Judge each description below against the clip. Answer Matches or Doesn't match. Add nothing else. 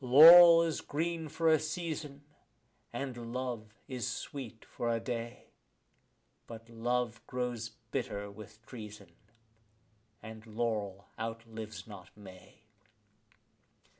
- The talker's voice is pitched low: Matches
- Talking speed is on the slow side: Matches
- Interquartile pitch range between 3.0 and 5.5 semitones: Matches